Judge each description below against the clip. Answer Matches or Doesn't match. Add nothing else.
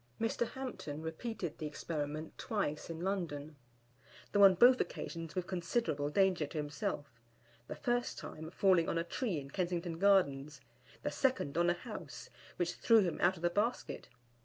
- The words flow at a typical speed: Matches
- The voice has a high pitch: Doesn't match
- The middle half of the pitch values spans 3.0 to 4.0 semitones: Doesn't match